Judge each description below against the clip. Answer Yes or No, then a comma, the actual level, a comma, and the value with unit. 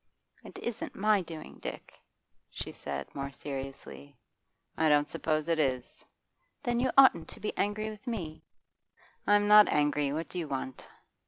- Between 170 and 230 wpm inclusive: No, average, 155 wpm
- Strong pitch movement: Yes, wide, 6.6 semitones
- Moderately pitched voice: Yes, medium, 160 Hz